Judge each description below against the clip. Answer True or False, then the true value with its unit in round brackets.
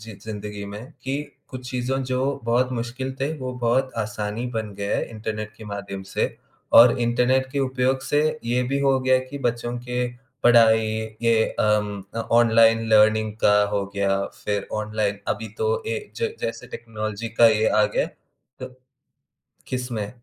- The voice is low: True (115 Hz)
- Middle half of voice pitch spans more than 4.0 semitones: False (3.0 semitones)